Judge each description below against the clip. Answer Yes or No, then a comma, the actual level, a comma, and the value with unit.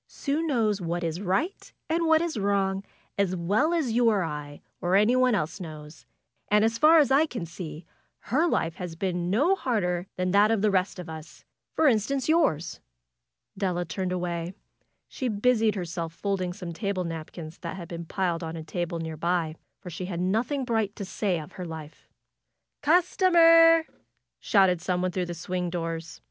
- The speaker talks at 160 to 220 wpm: Yes, average, 180 wpm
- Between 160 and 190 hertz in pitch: Yes, medium, 185 Hz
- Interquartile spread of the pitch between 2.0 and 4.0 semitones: No, average, 5.3 semitones